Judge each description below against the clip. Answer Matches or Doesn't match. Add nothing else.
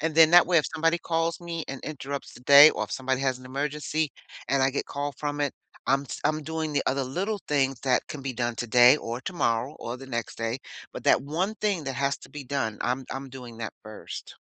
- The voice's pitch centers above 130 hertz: Matches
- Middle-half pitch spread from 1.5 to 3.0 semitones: Doesn't match